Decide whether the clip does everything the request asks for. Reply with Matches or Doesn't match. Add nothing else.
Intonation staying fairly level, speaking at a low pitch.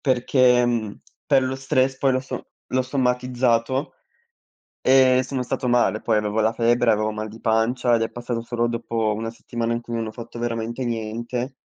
Matches